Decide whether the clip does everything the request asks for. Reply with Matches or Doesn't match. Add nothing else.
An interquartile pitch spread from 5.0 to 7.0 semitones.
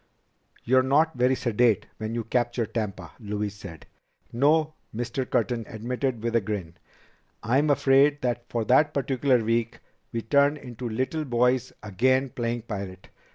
Doesn't match